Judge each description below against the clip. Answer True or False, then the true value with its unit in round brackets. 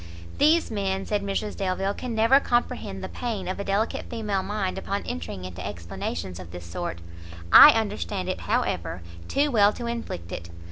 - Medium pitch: False (200 Hz)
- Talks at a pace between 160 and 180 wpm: True (175 wpm)